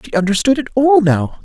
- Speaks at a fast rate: Yes, fast, 210 wpm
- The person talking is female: Yes, female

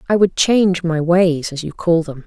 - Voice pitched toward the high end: No, medium, 170 Hz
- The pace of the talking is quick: Yes, fast, 240 wpm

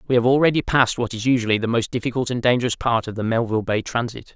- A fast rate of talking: Yes, fast, 250 wpm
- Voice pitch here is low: Yes, low, 120 Hz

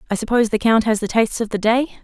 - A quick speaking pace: Yes, fast, 295 wpm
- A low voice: No, high, 225 Hz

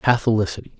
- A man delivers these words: Yes, male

